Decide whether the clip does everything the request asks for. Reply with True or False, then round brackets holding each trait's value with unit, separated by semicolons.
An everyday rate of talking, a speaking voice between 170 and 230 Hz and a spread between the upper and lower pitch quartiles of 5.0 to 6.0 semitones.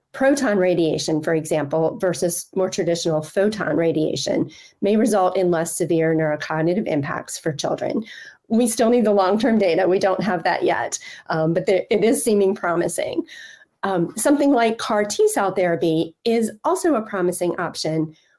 True (160 wpm; 185 Hz; 5.5 semitones)